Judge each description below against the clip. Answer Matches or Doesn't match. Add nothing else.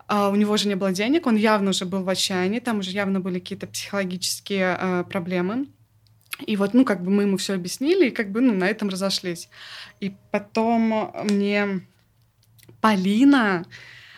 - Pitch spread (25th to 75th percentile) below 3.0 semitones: Matches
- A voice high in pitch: Matches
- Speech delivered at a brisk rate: Matches